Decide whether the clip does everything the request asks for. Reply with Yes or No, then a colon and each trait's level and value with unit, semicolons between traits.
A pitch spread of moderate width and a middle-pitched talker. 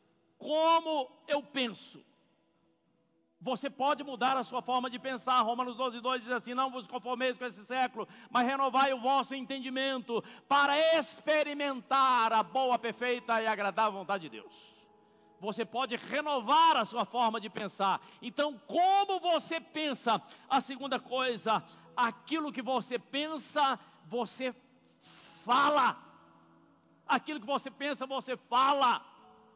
No: average, 3.1 semitones; very high, 255 Hz